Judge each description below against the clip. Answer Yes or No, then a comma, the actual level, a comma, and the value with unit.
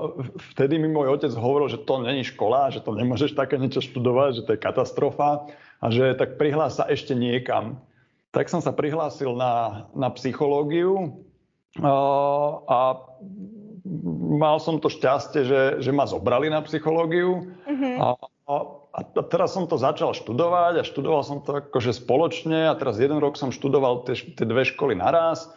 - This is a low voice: No, medium, 145 Hz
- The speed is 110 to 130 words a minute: No, fast, 165 wpm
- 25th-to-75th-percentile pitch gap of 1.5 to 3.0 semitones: No, average, 3.4 semitones